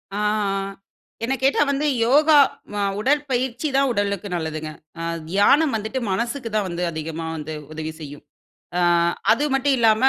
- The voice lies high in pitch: Yes, high, 220 Hz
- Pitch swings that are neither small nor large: No, wide, 8.3 semitones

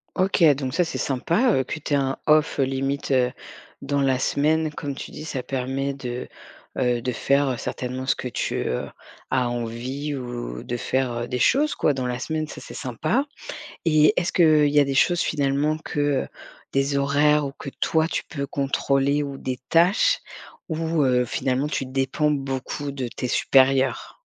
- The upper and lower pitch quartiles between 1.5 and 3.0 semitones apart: Yes, narrow, 2.6 semitones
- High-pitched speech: No, medium, 140 Hz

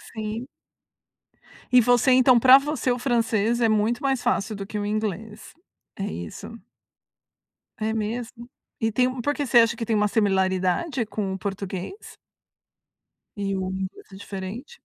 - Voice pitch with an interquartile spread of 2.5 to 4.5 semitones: Yes, average, 3.6 semitones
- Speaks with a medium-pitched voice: No, high, 220 Hz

